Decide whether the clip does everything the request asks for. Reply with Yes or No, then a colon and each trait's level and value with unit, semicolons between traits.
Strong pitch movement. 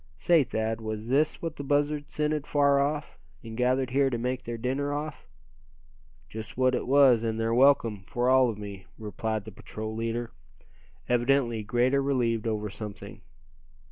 No: average, 3.9 semitones